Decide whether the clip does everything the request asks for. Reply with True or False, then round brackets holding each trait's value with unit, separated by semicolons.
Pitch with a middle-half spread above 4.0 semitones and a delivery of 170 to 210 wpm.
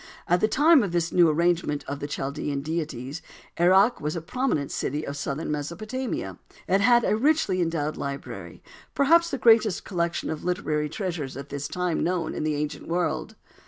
True (5.3 semitones; 175 wpm)